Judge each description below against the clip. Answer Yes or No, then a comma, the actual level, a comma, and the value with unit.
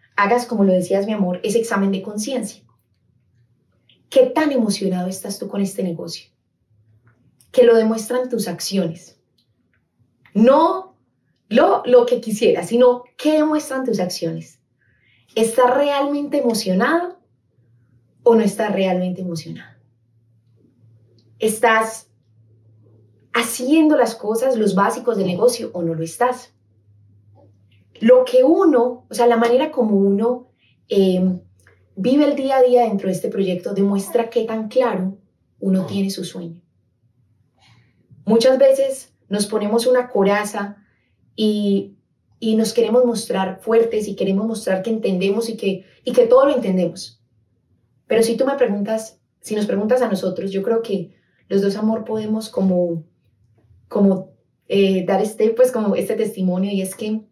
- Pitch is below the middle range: No, high, 200 Hz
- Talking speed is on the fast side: No, average, 140 wpm